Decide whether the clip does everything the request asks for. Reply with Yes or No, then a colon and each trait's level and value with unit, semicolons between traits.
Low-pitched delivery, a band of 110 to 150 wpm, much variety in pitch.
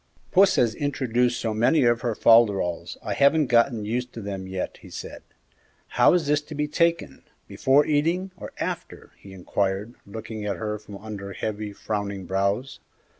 No: low, 115 Hz; average, 170 wpm; wide, 5.8 semitones